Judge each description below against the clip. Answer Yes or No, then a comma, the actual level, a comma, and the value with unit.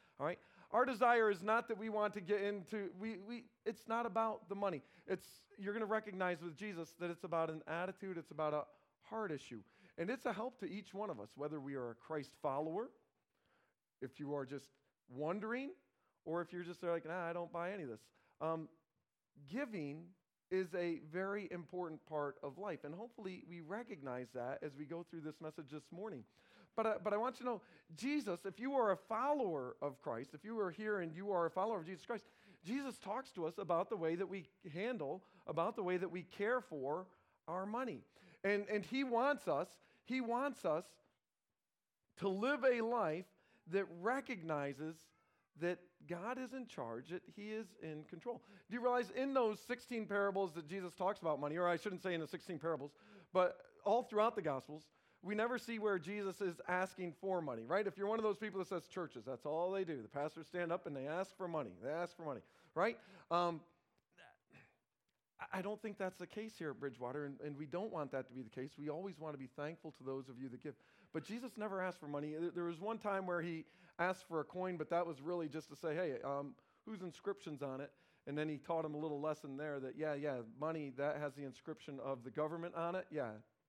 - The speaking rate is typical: No, fast, 220 wpm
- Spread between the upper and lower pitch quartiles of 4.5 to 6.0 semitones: Yes, average, 5.2 semitones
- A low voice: No, medium, 175 Hz